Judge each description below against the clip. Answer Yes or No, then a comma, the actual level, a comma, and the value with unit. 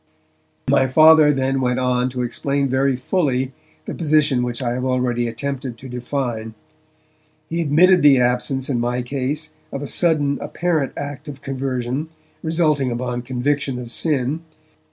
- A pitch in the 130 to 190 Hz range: Yes, low, 135 Hz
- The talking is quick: No, average, 150 wpm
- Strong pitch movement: No, average, 2.8 semitones